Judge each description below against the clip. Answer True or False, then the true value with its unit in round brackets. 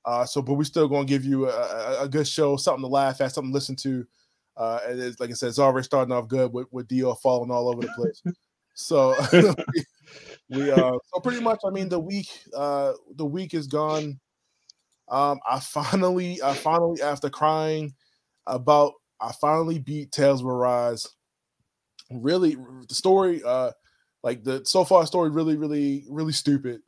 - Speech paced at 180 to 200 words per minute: True (185 wpm)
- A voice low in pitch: False (145 Hz)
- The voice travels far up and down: False (4.0 semitones)